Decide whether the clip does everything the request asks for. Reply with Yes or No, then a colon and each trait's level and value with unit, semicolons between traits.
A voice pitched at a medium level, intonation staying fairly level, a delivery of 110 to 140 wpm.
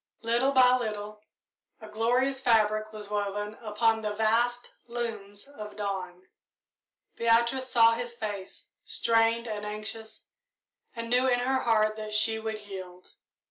No: high, 220 Hz; narrow, 2.1 semitones; slow, 135 wpm